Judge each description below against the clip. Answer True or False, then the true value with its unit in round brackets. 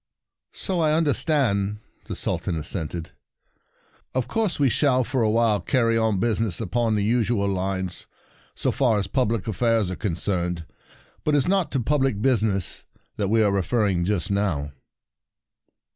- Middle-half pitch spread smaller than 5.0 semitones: True (4.5 semitones)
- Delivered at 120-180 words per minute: True (165 wpm)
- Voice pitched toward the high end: False (110 Hz)